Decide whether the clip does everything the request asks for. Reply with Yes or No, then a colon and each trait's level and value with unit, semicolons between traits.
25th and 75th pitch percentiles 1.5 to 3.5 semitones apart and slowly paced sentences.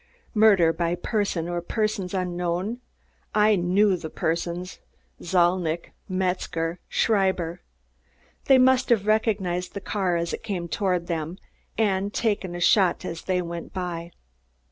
Yes: average, 2.9 semitones; slow, 130 wpm